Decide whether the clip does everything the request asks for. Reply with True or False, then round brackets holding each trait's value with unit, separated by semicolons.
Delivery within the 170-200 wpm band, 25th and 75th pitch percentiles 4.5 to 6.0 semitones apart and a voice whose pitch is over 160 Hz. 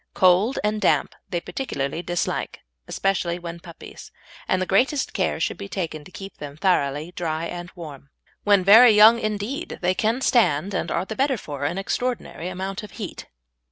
False (175 wpm; 3.9 semitones; 185 Hz)